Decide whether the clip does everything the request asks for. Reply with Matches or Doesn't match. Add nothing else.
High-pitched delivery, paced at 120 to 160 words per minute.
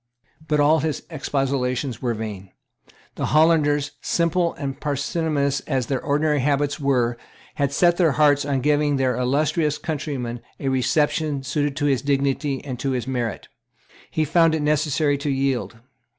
Doesn't match